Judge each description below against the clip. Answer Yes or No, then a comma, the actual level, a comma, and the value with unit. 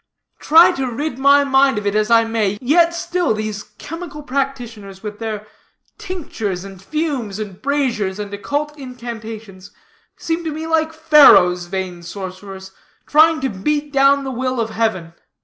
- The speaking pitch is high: Yes, high, 240 Hz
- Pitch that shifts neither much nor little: No, wide, 6.3 semitones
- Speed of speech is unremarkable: Yes, average, 155 wpm